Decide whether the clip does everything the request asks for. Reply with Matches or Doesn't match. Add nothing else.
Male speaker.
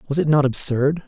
Matches